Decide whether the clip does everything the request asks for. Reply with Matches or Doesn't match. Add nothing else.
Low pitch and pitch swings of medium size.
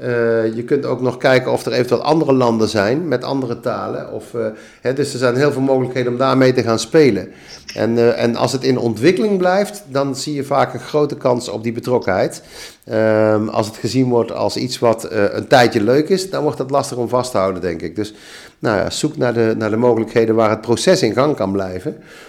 Matches